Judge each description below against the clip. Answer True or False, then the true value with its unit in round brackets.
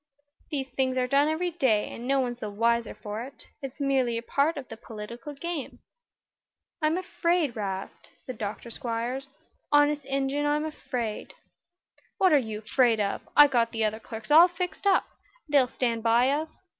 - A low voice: False (260 Hz)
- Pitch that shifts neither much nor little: True (4.2 semitones)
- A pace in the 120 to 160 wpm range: False (170 wpm)